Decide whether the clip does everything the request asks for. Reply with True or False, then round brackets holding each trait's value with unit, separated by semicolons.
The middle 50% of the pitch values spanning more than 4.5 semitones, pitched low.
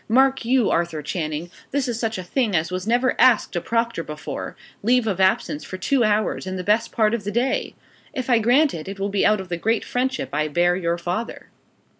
False (5.3 semitones; 210 Hz)